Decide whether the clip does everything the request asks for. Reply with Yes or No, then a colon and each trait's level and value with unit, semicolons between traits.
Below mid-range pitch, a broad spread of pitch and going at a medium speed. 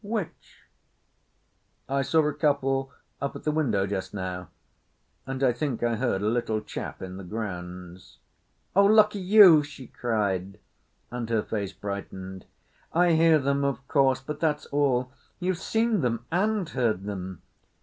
Yes: low, 130 Hz; wide, 7.1 semitones; average, 150 wpm